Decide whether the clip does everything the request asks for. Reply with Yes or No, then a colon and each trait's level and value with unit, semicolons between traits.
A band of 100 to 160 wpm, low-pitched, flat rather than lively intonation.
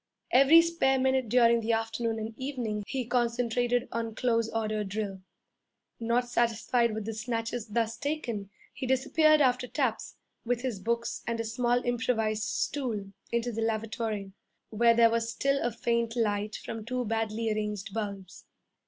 No: average, 155 wpm; high, 230 Hz; narrow, 2.0 semitones